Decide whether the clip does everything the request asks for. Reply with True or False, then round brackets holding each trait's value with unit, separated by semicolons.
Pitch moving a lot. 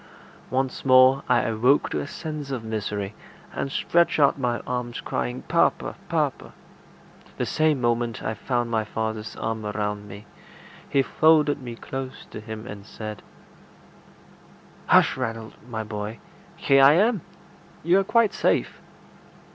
False (4.2 semitones)